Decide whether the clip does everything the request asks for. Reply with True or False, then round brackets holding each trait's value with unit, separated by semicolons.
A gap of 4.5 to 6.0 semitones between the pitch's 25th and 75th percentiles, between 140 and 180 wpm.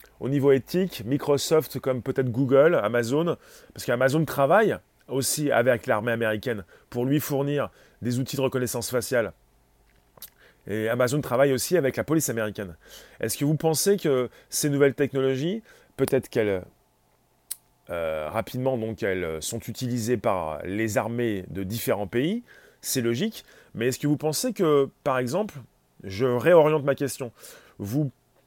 False (3.6 semitones; 145 wpm)